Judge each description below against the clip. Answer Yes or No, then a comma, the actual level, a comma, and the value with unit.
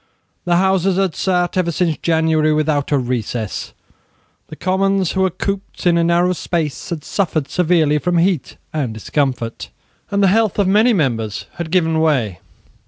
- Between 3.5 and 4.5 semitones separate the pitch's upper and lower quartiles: Yes, average, 3.9 semitones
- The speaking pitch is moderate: Yes, medium, 170 Hz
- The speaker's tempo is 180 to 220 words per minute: No, average, 170 wpm